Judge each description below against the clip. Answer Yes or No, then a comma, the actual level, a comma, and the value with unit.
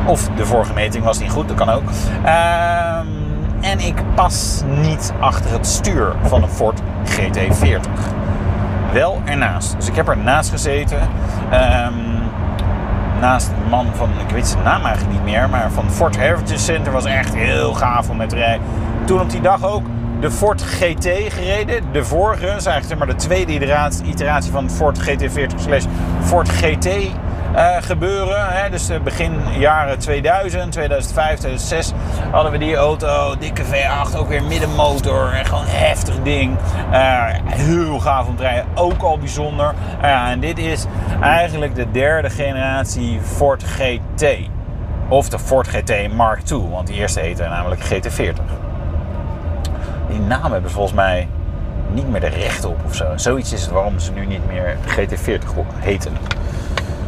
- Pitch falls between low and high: No, very low, 95 Hz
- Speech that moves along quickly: No, average, 160 wpm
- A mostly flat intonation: No, average, 3.8 semitones